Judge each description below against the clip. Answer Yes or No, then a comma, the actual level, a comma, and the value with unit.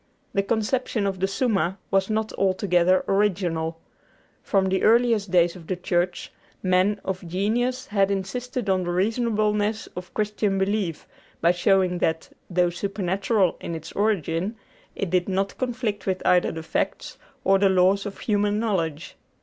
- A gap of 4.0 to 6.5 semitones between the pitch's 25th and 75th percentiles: No, average, 2.7 semitones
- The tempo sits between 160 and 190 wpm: No, average, 150 wpm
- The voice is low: No, high, 195 Hz